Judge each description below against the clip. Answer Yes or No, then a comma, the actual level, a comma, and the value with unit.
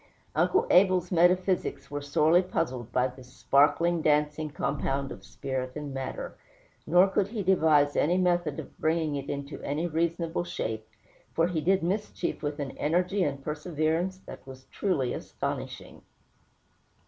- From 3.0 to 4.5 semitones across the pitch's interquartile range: Yes, average, 3.9 semitones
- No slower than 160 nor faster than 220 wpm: No, average, 145 wpm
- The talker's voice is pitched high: No, medium, 155 Hz